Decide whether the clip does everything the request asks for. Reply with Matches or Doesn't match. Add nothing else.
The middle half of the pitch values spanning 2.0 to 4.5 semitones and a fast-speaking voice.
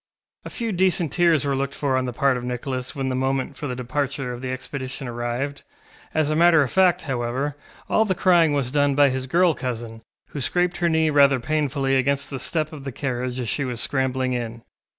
Matches